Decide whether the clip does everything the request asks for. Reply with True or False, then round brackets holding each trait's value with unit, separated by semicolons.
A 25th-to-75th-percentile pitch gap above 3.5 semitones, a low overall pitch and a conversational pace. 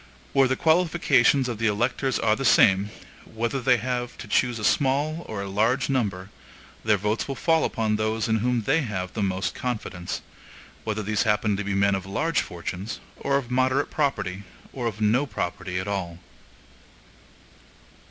True (4.5 semitones; 110 Hz; 170 wpm)